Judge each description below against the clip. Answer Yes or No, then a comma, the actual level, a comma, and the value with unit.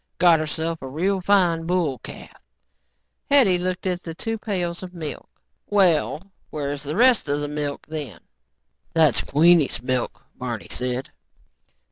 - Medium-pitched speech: Yes, medium, 165 Hz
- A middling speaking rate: Yes, average, 145 wpm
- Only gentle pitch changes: No, average, 4.1 semitones